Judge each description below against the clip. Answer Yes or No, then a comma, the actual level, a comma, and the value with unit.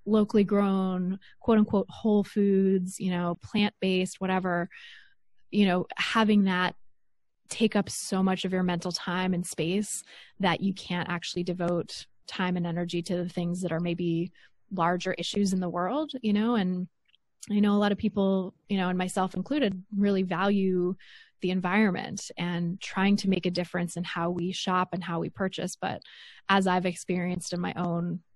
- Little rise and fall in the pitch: Yes, narrow, 2.3 semitones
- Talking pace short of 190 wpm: Yes, average, 175 wpm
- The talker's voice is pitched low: No, medium, 185 Hz